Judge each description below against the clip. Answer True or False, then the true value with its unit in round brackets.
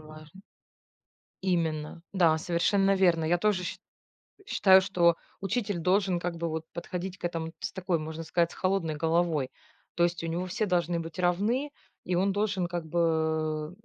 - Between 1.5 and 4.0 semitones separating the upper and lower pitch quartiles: True (2.5 semitones)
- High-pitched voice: False (175 Hz)